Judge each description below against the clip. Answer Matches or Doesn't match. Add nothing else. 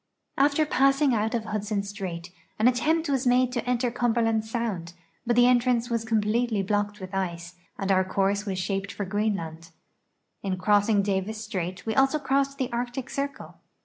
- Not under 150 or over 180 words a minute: Matches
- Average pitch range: Matches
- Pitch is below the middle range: Doesn't match